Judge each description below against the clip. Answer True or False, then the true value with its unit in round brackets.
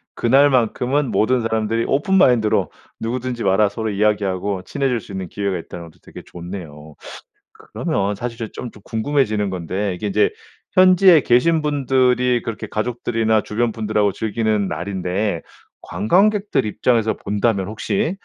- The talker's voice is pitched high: False (110 Hz)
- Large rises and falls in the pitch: False (4.0 semitones)